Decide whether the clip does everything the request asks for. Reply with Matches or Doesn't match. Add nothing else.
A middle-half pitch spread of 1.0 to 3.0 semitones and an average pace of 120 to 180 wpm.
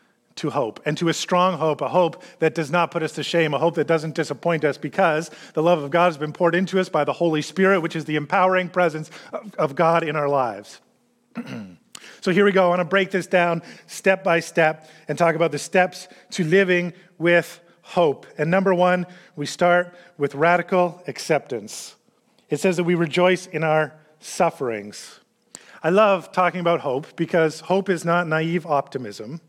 Doesn't match